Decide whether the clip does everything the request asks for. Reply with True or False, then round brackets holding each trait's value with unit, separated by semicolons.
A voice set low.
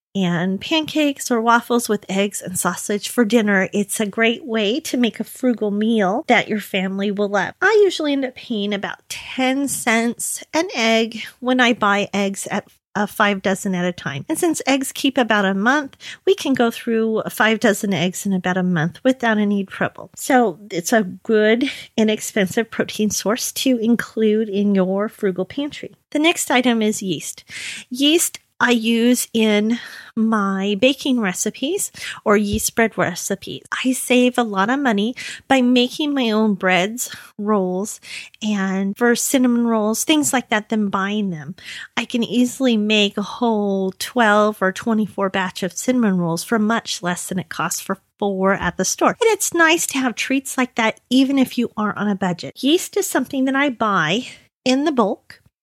False (220 Hz)